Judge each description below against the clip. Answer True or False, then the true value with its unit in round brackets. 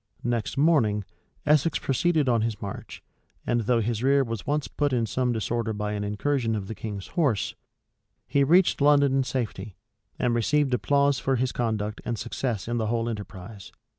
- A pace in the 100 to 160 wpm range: False (175 wpm)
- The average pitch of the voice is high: False (120 Hz)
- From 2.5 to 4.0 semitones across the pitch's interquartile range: False (4.4 semitones)